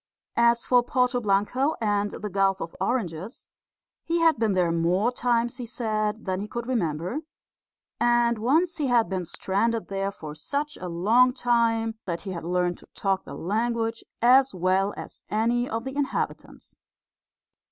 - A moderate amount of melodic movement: Yes, average, 4.2 semitones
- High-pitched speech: Yes, high, 225 Hz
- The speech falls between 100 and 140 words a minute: No, average, 165 wpm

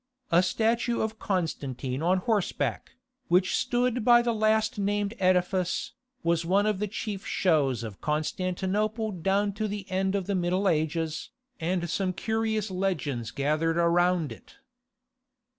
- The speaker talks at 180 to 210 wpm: No, average, 140 wpm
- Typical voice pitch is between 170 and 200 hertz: Yes, medium, 185 Hz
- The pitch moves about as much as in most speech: Yes, average, 4.0 semitones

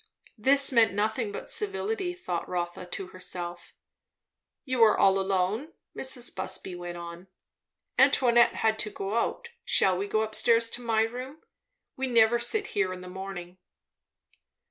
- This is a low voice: No, high, 220 Hz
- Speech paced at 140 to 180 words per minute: Yes, average, 150 wpm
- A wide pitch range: No, average, 4.9 semitones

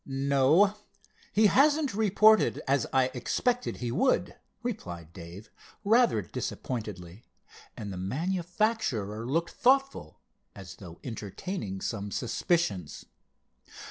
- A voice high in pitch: No, low, 135 Hz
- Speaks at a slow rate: Yes, slow, 100 wpm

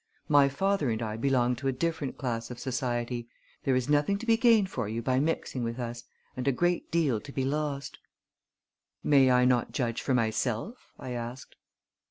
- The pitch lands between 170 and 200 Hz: No, low, 130 Hz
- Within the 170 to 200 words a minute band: Yes, average, 190 wpm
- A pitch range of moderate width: Yes, average, 3.5 semitones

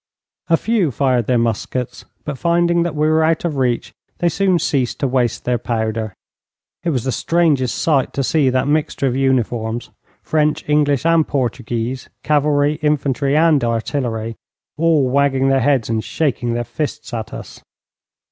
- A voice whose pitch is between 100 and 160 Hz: Yes, low, 135 Hz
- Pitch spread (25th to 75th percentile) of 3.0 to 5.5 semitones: Yes, average, 4.1 semitones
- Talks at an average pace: Yes, average, 160 wpm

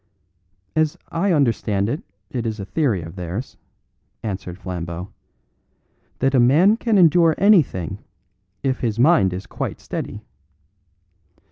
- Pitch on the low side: Yes, low, 120 Hz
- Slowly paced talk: Yes, slow, 125 wpm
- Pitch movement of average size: No, wide, 8.8 semitones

